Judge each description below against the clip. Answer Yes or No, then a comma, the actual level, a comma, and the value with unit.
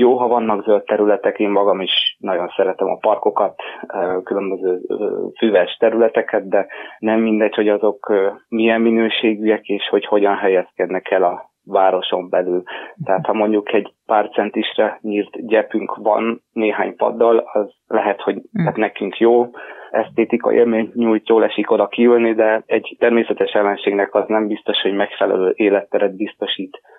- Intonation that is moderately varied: No, narrow, 2.0 semitones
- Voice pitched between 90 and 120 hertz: Yes, low, 110 Hz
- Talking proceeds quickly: No, average, 145 wpm